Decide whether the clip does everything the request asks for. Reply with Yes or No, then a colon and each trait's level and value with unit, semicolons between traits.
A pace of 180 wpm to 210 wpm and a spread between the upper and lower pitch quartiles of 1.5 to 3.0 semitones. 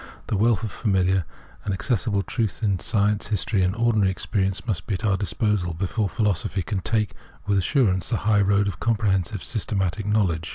Yes: average, 190 wpm; narrow, 2.5 semitones